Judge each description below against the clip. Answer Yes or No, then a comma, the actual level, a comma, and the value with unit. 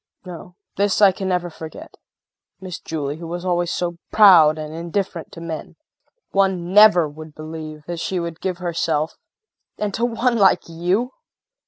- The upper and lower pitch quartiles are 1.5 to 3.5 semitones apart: Yes, average, 3.0 semitones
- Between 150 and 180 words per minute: Yes, average, 160 wpm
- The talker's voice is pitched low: No, medium, 175 Hz